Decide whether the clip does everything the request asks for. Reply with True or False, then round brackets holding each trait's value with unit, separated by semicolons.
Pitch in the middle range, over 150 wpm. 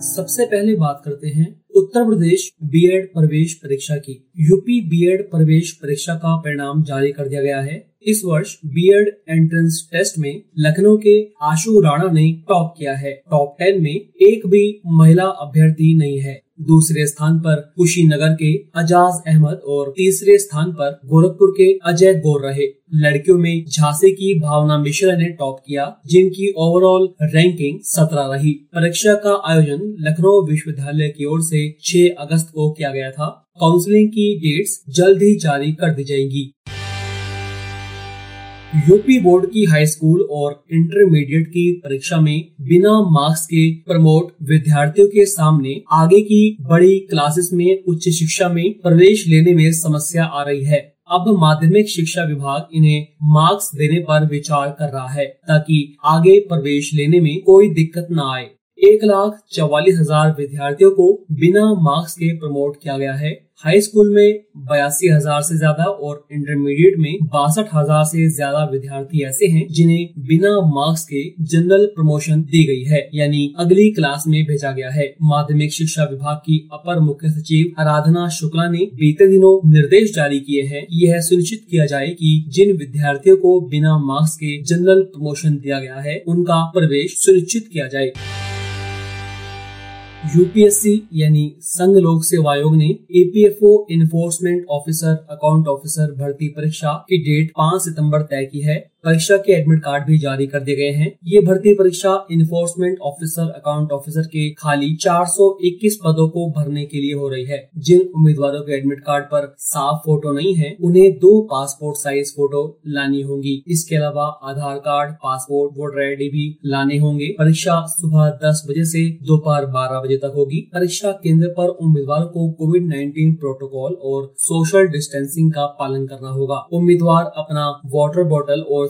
True (155 Hz; 160 wpm)